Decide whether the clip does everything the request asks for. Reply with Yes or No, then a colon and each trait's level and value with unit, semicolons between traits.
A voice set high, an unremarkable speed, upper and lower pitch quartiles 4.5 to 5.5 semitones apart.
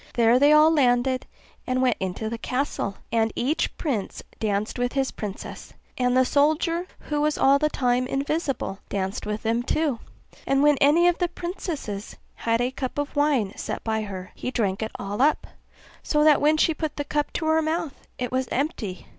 Yes: very high, 260 Hz; average, 190 wpm; average, 4.9 semitones